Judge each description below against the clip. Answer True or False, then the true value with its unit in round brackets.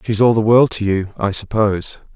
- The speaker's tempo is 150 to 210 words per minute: False (225 wpm)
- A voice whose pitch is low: True (105 Hz)